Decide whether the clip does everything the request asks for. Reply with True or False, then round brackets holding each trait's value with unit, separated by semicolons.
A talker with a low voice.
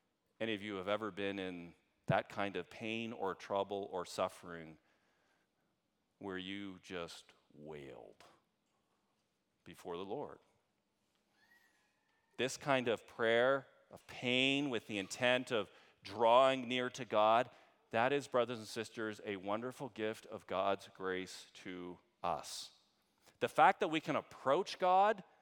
True (105 Hz)